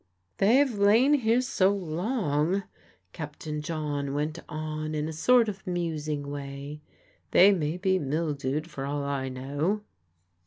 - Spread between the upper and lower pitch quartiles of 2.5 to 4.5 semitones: No, average, 5.1 semitones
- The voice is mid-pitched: Yes, medium, 155 Hz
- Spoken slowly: Yes, slow, 130 wpm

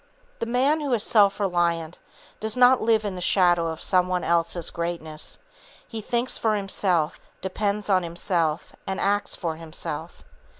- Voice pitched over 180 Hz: Yes, high, 190 Hz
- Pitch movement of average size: Yes, average, 4.1 semitones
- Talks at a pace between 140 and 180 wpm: Yes, average, 160 wpm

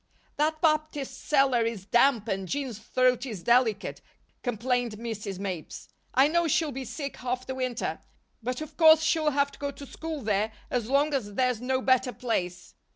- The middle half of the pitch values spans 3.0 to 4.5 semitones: Yes, average, 3.9 semitones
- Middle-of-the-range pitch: No, very high, 255 Hz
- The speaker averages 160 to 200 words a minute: Yes, average, 175 wpm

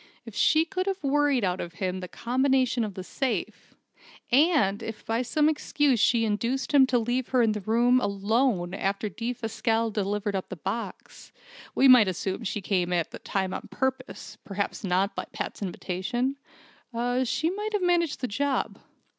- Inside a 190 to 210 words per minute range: No, average, 170 wpm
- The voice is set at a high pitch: Yes, high, 230 Hz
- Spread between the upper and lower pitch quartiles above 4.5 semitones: Yes, average, 5.1 semitones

